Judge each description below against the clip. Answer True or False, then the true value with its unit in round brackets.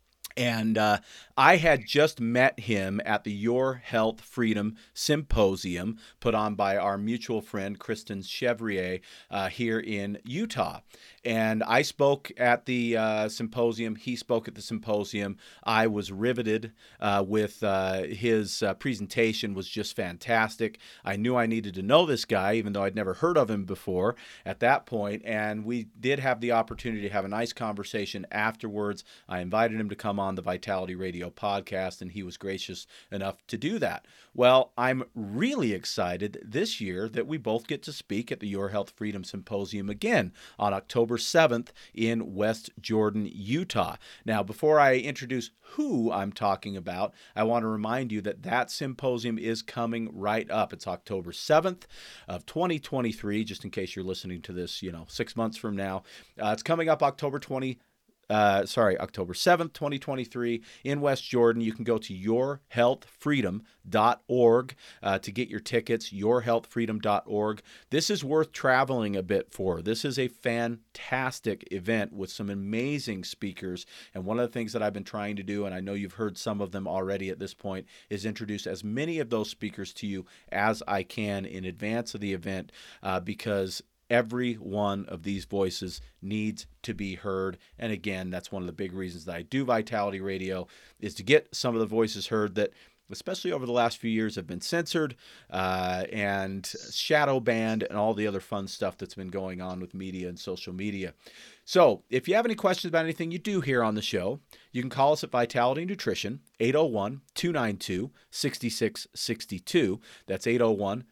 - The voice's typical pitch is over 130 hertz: False (110 Hz)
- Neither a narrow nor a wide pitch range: True (3.4 semitones)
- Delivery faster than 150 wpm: True (180 wpm)